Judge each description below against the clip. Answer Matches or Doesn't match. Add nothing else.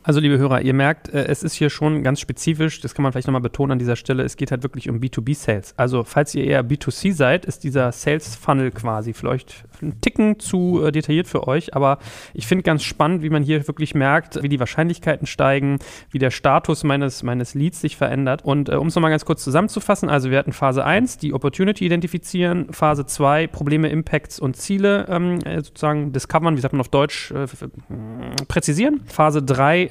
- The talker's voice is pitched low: Doesn't match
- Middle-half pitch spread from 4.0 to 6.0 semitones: Doesn't match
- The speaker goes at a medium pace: Doesn't match